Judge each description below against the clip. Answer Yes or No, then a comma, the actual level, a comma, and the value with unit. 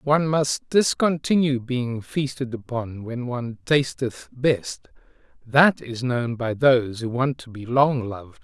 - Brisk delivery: No, average, 150 wpm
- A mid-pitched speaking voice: No, low, 125 Hz